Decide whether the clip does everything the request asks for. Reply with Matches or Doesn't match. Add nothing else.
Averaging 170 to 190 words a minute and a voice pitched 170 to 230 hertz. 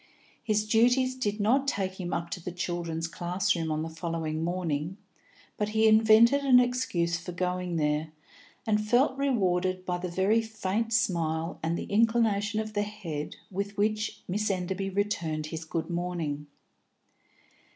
Doesn't match